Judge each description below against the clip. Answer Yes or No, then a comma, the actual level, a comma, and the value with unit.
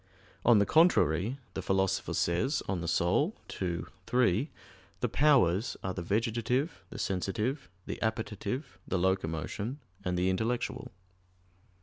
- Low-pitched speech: Yes, low, 100 Hz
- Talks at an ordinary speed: No, slow, 120 wpm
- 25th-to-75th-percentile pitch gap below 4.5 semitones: No, wide, 5.5 semitones